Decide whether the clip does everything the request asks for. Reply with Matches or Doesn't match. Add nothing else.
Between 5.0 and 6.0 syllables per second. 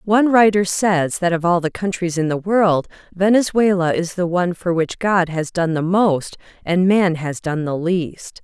Doesn't match